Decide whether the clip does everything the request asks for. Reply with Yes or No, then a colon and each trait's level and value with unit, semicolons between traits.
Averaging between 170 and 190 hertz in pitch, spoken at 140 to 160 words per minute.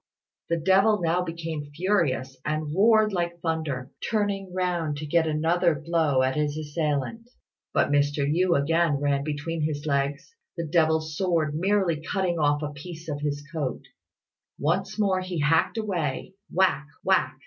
No: medium, 160 Hz; average, 150 wpm